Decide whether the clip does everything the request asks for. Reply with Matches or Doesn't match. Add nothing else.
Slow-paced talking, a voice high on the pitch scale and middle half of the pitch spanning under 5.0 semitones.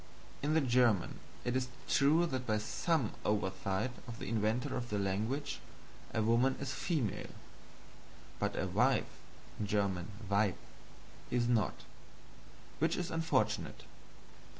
Doesn't match